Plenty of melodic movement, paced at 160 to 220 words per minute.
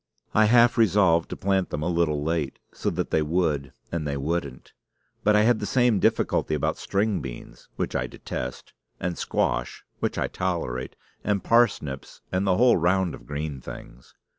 Yes: wide, 6.0 semitones; average, 175 wpm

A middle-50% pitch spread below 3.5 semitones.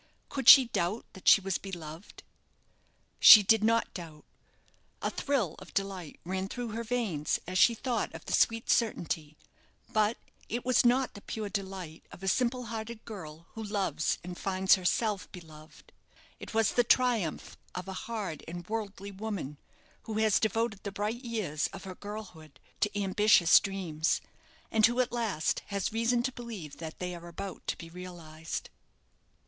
No: average, 4.5 semitones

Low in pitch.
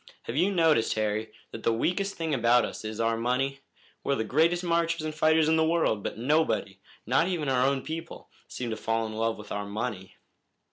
Yes: low, 130 Hz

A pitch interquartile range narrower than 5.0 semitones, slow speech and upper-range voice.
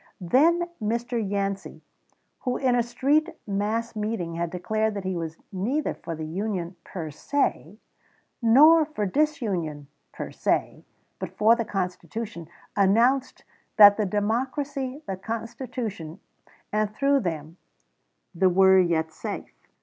No: average, 5.3 semitones; slow, 125 wpm; high, 210 Hz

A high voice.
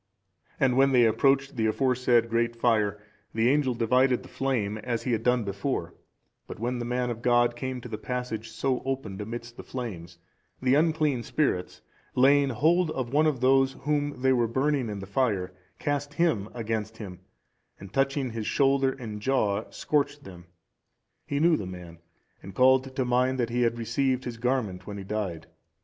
No: low, 125 Hz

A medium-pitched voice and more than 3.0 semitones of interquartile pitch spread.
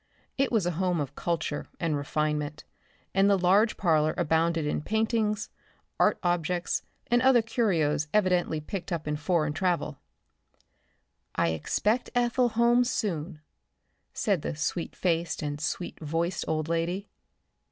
Yes: medium, 175 Hz; average, 5.2 semitones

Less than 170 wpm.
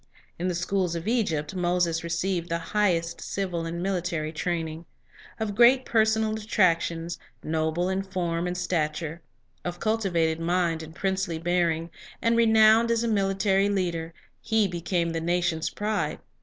Yes: average, 140 wpm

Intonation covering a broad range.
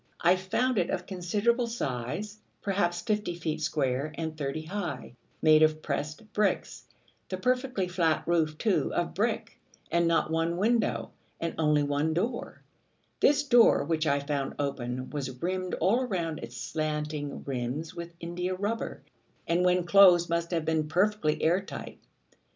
No: average, 4.2 semitones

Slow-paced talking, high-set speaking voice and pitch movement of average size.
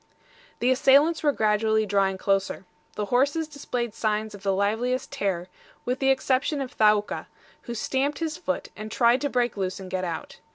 No: average, 175 wpm; high, 235 Hz; average, 4.8 semitones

